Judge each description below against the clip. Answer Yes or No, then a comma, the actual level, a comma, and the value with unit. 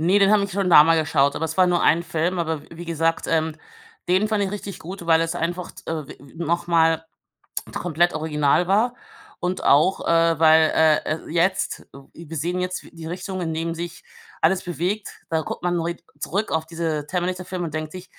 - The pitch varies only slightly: Yes, narrow, 2.2 semitones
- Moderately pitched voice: Yes, medium, 170 Hz